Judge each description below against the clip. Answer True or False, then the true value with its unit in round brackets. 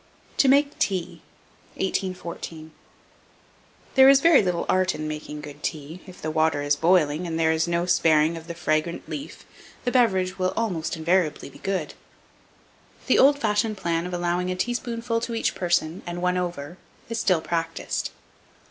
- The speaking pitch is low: False (175 Hz)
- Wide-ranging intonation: False (3.4 semitones)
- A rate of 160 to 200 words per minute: True (165 wpm)